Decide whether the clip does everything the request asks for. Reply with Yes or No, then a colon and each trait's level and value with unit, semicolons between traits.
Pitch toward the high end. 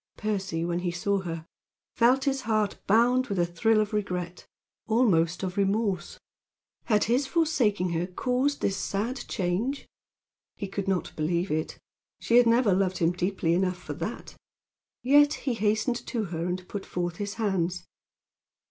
Yes: high, 200 Hz